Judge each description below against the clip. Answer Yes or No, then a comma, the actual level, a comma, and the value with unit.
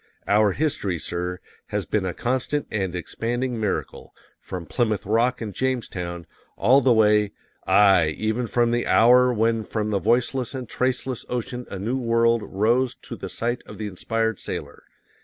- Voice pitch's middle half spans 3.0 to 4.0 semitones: Yes, average, 3.3 semitones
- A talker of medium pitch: No, low, 115 Hz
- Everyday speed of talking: Yes, average, 160 wpm